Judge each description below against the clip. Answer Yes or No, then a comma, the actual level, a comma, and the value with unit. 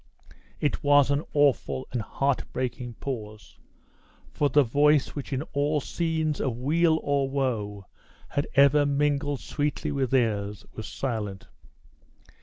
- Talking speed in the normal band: No, slow, 130 wpm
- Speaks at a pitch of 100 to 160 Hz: Yes, medium, 140 Hz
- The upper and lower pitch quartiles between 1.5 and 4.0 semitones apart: Yes, average, 3.1 semitones